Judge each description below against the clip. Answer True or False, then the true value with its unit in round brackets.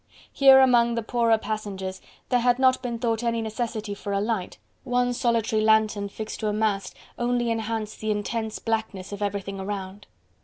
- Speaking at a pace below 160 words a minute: False (170 wpm)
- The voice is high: True (220 Hz)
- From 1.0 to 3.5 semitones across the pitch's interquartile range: True (2.5 semitones)